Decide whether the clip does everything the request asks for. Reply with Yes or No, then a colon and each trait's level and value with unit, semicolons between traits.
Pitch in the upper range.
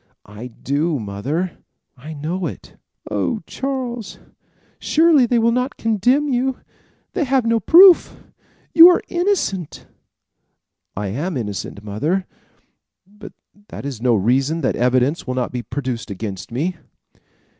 No: medium, 160 Hz